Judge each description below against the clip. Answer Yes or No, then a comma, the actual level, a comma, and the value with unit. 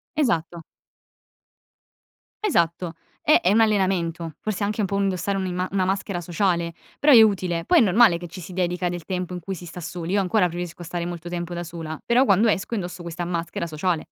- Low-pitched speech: No, medium, 180 Hz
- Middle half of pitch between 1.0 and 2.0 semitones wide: No, narrow, 2.5 semitones